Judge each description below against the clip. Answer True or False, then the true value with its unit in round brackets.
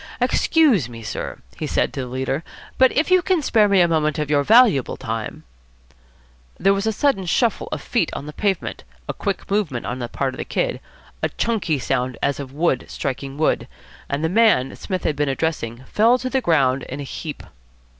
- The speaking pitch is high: False (155 Hz)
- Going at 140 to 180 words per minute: False (205 wpm)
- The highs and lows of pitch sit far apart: True (8.3 semitones)